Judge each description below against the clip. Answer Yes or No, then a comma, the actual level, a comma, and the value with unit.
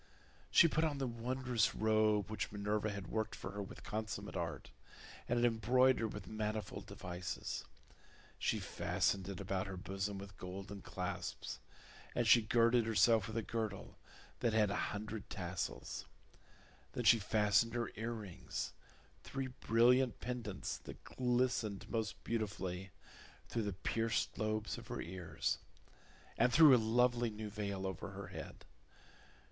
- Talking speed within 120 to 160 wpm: Yes, average, 140 wpm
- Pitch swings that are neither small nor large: Yes, average, 3.0 semitones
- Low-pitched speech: Yes, low, 110 Hz